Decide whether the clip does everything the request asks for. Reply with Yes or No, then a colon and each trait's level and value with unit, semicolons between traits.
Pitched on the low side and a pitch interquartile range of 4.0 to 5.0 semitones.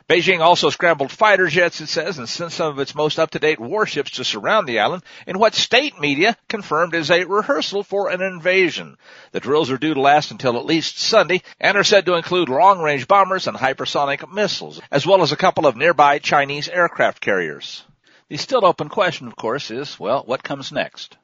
No: medium, 170 Hz; average, 4.4 semitones